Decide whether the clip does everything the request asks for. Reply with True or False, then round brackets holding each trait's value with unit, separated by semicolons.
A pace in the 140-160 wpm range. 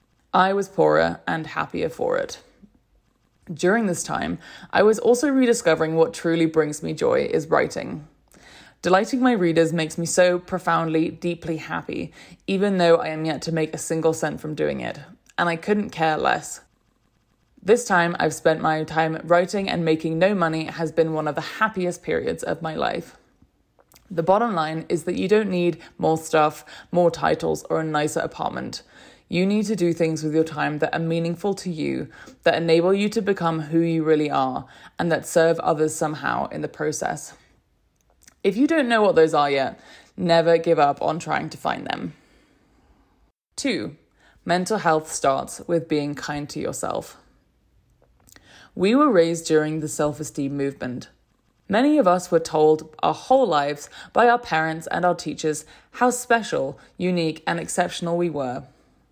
False (170 wpm)